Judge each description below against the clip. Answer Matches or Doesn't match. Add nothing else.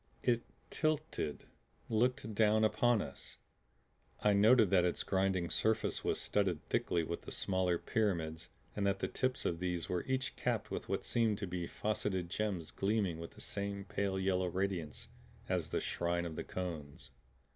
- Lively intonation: Doesn't match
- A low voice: Matches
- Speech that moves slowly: Doesn't match